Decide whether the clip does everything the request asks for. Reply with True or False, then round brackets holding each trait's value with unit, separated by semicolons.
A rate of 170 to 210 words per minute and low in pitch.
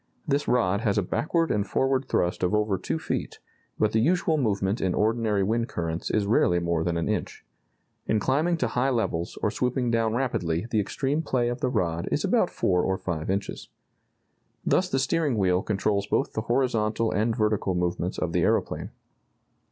True (185 wpm; 110 Hz)